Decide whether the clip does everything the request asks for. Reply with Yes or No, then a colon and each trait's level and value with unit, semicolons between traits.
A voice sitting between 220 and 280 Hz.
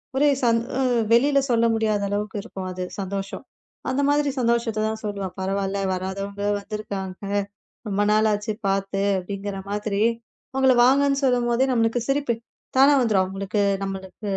No: high, 210 Hz